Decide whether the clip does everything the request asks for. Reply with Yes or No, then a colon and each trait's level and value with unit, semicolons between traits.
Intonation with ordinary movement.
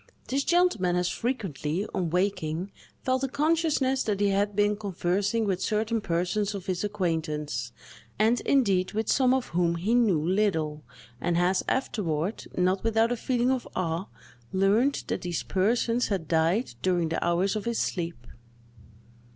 Yes: average, 4.8 semitones